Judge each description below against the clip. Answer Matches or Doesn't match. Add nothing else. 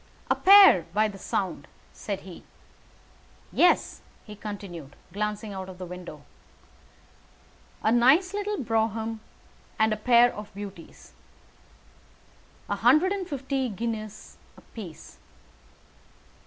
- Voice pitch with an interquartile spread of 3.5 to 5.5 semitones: Matches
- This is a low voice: Doesn't match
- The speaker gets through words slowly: Matches